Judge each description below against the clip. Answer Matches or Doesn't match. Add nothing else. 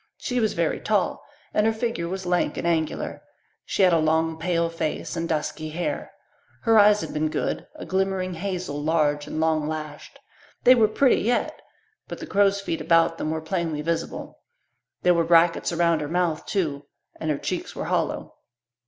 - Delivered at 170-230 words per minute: Matches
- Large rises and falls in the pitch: Doesn't match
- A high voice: Doesn't match